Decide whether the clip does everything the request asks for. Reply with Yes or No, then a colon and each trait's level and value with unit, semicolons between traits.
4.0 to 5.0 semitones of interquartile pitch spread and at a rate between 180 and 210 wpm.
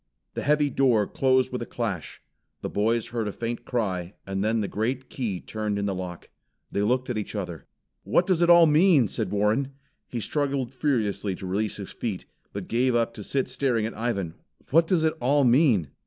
Yes: average, 4.7 semitones; average, 200 wpm